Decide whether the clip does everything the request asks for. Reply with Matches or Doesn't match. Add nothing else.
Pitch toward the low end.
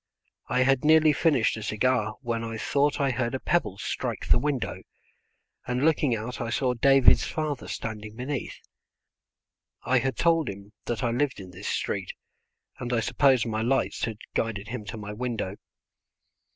Matches